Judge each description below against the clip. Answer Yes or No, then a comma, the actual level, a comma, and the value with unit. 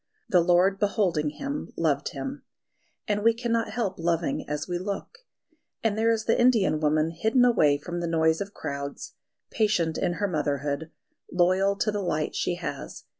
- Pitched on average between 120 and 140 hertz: No, medium, 180 Hz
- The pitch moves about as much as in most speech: Yes, average, 5.0 semitones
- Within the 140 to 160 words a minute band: No, average, 170 wpm